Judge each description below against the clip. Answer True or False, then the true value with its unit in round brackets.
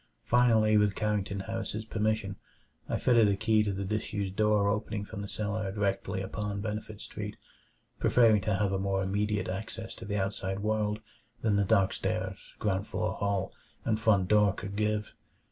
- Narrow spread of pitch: True (1.5 semitones)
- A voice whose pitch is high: False (105 Hz)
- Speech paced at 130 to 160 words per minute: False (170 wpm)